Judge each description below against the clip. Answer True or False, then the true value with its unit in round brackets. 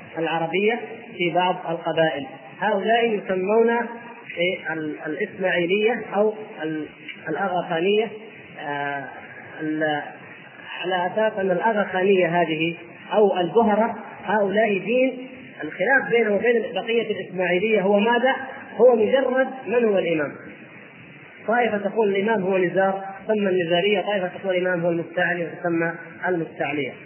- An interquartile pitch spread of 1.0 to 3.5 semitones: False (4.2 semitones)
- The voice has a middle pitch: False (195 Hz)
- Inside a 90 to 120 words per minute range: True (100 wpm)